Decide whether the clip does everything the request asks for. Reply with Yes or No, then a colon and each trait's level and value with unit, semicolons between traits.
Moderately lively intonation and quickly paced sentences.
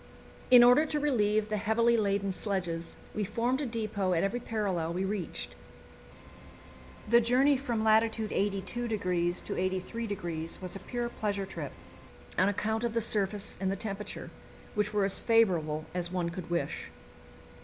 No: average, 3.6 semitones; average, 155 wpm